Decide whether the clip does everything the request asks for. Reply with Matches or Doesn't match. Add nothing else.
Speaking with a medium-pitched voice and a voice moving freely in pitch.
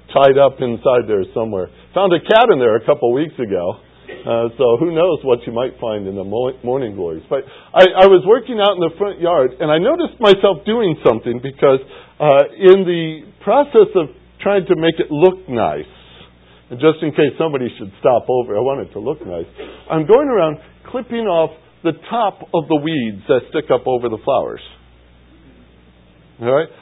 Matches